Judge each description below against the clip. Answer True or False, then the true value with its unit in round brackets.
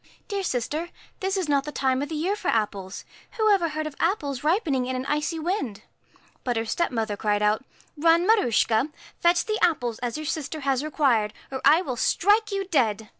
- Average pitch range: False (6.2 semitones)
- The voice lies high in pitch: True (295 Hz)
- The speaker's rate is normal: False (210 wpm)